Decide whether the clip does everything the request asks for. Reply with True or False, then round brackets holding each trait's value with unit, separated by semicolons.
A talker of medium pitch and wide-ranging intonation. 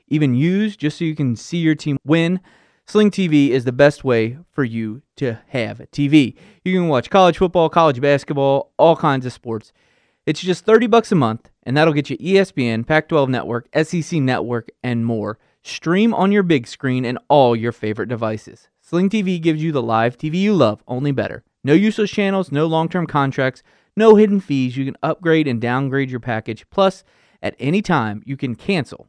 True (145 Hz; 6.0 semitones)